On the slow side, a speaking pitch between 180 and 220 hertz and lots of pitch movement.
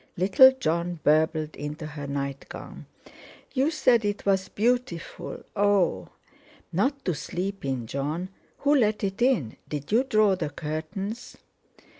Yes: slow, 130 wpm; medium, 185 Hz; wide, 6.1 semitones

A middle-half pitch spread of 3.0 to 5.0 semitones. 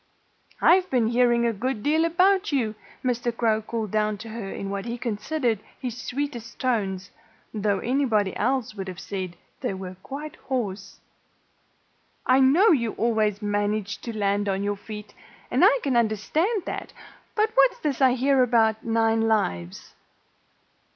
Yes: average, 4.1 semitones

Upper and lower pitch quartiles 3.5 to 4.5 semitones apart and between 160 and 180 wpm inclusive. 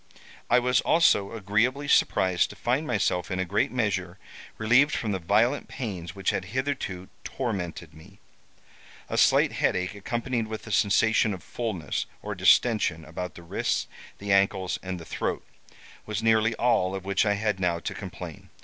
Yes: average, 4.1 semitones; average, 165 wpm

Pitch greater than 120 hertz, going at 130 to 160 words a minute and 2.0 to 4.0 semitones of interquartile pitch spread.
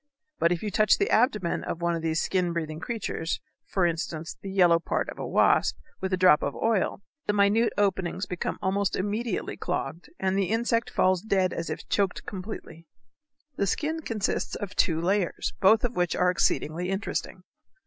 No: high, 190 Hz; average, 180 wpm; average, 3.4 semitones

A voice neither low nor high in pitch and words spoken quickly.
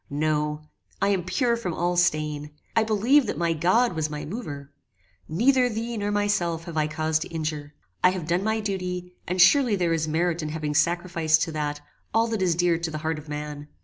Yes: medium, 170 Hz; fast, 210 wpm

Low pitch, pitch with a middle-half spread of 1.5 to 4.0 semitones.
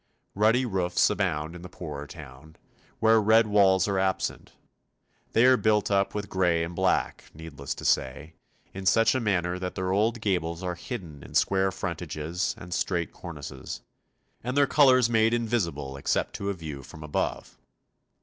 No: very low, 95 Hz; average, 4.6 semitones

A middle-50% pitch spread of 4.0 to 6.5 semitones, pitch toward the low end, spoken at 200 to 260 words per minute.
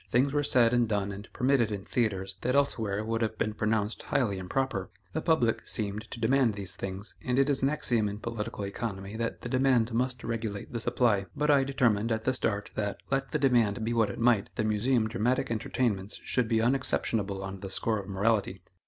No: average, 3.5 semitones; low, 115 Hz; fast, 205 wpm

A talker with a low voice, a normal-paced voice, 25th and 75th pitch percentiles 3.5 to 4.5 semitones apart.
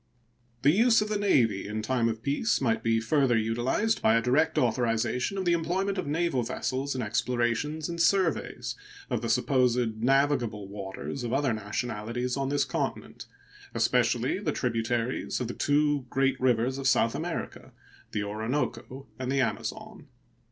Yes: low, 125 Hz; average, 160 wpm; average, 4.1 semitones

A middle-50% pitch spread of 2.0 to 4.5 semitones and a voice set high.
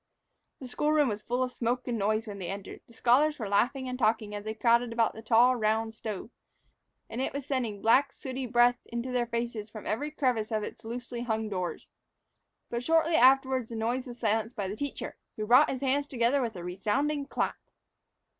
Yes: average, 2.9 semitones; high, 235 Hz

